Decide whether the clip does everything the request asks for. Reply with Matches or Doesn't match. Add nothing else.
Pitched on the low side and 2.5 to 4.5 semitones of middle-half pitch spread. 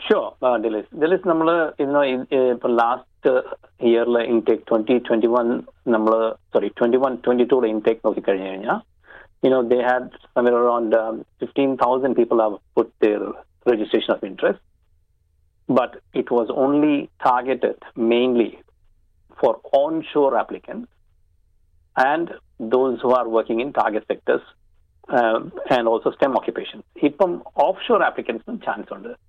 Matches